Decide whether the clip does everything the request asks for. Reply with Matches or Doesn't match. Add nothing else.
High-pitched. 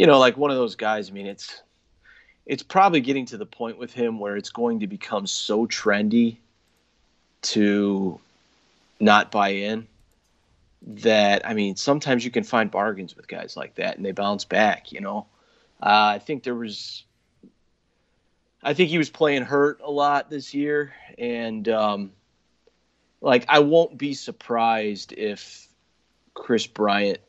Doesn't match